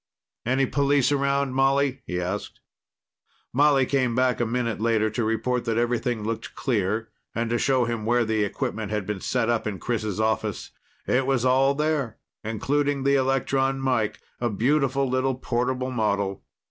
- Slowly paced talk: No, average, 160 wpm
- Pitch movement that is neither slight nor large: Yes, average, 3.4 semitones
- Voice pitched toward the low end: Yes, low, 125 Hz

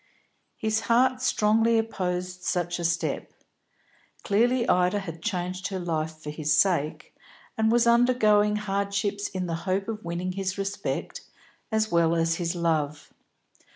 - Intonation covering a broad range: No, average, 4.2 semitones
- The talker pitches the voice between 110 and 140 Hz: No, high, 190 Hz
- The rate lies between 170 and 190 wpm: No, average, 140 wpm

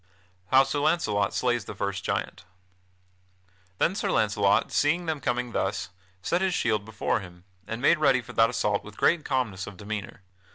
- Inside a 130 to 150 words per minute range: No, average, 175 wpm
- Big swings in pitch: Yes, wide, 5.9 semitones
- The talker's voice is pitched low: Yes, low, 115 Hz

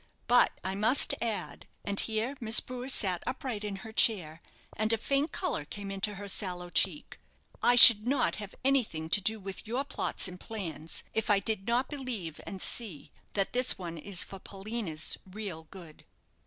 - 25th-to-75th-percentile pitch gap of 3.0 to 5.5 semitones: Yes, average, 4.0 semitones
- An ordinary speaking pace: Yes, average, 180 wpm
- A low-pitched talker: No, high, 205 Hz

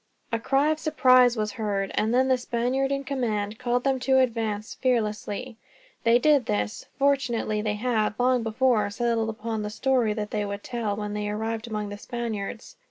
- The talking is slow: No, average, 180 wpm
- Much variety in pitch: No, average, 3.2 semitones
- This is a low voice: No, high, 230 Hz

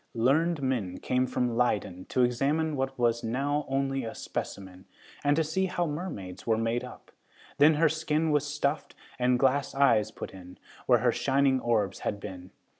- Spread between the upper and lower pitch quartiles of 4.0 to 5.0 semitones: Yes, average, 4.4 semitones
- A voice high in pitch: No, low, 130 Hz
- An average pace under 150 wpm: No, average, 175 wpm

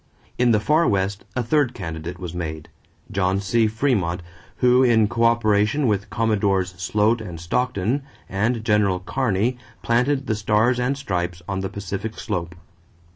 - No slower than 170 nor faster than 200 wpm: No, average, 145 wpm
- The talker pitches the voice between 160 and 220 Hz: No, low, 105 Hz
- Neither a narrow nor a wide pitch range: Yes, average, 4.2 semitones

